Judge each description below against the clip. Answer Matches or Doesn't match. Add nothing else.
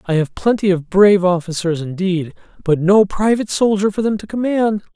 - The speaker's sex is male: Matches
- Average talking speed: Matches